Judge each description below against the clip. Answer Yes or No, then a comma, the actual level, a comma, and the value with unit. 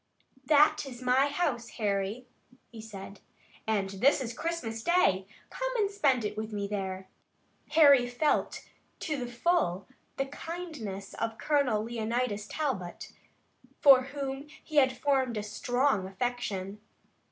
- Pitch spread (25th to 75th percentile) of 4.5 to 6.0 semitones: Yes, wide, 5.4 semitones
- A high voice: Yes, high, 245 Hz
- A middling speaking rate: No, slow, 130 wpm